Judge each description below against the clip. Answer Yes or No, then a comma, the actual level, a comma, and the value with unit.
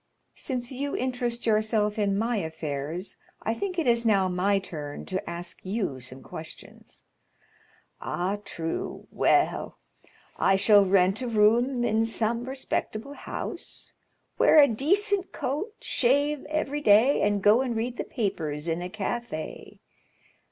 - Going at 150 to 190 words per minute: No, slow, 135 wpm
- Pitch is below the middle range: No, high, 220 Hz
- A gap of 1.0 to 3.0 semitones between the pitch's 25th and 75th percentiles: No, average, 5.1 semitones